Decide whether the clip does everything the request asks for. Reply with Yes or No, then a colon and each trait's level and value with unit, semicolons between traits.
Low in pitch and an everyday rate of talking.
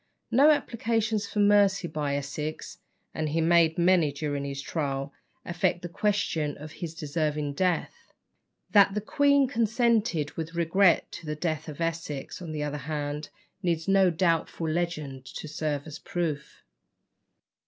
No: medium, 165 Hz; average, 145 wpm